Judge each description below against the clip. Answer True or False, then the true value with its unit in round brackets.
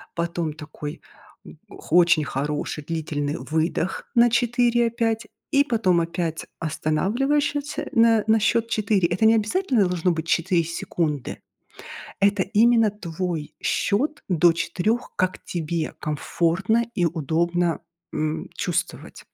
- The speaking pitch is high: False (180 Hz)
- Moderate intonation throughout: False (5.7 semitones)